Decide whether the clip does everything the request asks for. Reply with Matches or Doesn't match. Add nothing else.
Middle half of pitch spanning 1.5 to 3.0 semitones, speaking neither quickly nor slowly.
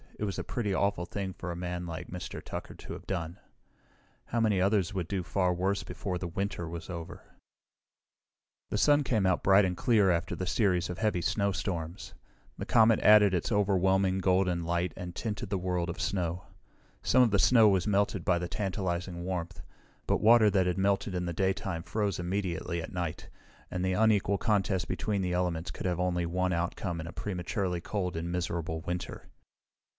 Matches